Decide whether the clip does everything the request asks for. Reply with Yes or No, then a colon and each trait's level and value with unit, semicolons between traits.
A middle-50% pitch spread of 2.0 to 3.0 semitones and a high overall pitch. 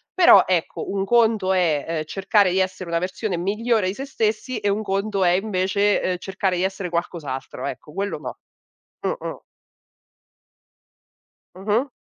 Yes: average, 2.7 semitones; high, 195 Hz